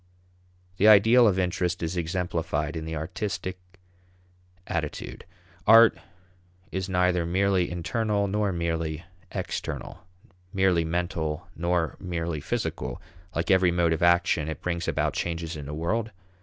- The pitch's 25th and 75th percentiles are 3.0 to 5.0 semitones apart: No, narrow, 2.6 semitones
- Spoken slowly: Yes, slow, 130 wpm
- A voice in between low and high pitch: No, very low, 85 Hz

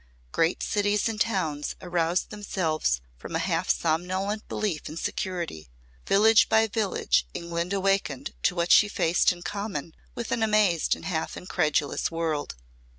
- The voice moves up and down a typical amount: Yes, average, 4.2 semitones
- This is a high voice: No, medium, 180 Hz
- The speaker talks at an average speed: Yes, average, 145 wpm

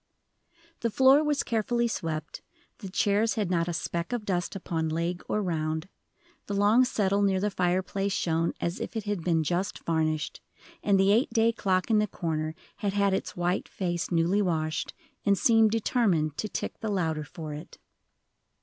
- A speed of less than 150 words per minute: No, average, 175 wpm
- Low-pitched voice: No, high, 190 Hz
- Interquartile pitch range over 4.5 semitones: No, average, 4.1 semitones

